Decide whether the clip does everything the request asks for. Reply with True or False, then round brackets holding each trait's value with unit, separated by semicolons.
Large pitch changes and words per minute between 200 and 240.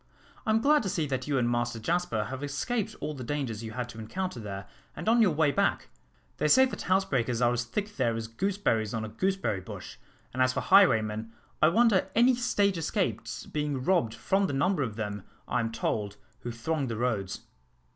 True (8.6 semitones; 205 wpm)